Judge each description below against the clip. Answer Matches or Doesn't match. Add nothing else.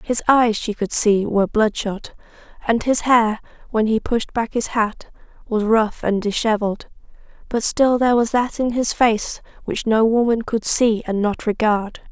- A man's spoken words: Doesn't match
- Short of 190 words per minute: Matches